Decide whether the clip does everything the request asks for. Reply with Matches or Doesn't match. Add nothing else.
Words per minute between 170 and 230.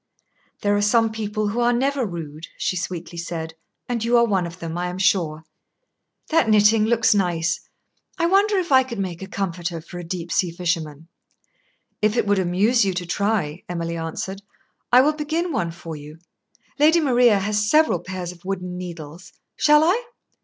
Matches